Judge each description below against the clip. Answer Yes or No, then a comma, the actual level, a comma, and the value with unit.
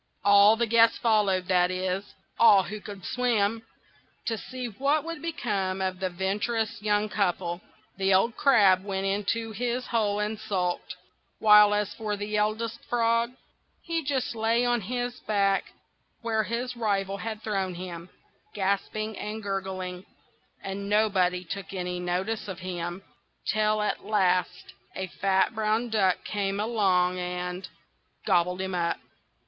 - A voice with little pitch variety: No, average, 3.0 semitones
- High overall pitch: Yes, high, 205 Hz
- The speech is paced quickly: No, slow, 135 wpm